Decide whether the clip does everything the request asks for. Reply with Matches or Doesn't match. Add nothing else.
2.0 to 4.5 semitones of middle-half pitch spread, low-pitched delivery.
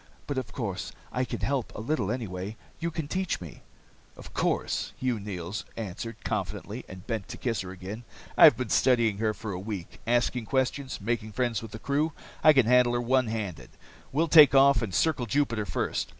Matches